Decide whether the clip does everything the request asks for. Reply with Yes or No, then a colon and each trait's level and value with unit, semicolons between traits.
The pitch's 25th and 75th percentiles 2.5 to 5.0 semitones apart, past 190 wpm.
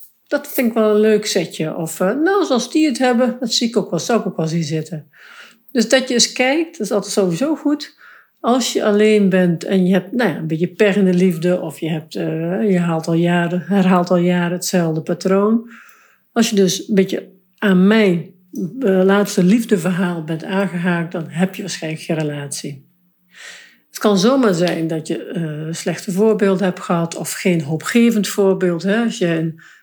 Yes: average, 3.8 semitones; fast, 200 wpm